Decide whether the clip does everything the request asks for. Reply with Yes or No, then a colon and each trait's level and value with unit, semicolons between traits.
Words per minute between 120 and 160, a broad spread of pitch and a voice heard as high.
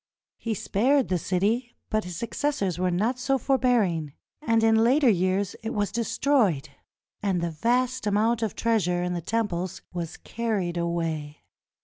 No: average, 155 wpm; average, 4.9 semitones; high, 210 Hz